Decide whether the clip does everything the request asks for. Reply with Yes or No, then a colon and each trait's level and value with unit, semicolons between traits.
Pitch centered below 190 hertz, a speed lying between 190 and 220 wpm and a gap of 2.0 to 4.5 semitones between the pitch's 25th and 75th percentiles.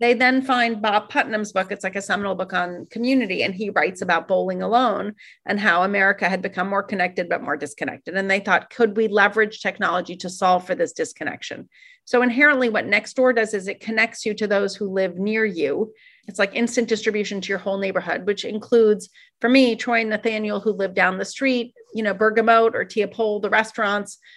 No: high, 210 Hz; fast, 205 wpm; average, 2.9 semitones